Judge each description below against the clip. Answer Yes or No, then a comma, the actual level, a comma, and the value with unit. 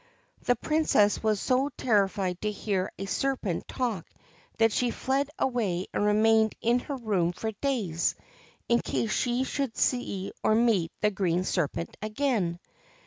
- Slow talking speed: No, average, 145 wpm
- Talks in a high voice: Yes, high, 215 Hz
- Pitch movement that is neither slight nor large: Yes, average, 4.3 semitones